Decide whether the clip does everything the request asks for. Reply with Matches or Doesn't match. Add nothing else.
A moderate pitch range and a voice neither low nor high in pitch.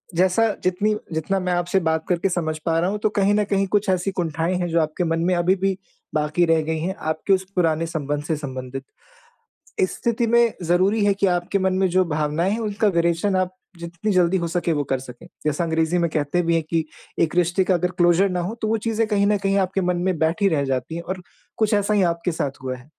Matches